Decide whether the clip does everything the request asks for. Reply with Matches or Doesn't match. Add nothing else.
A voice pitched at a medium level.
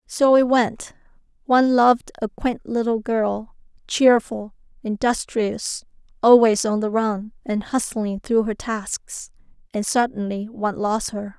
Doesn't match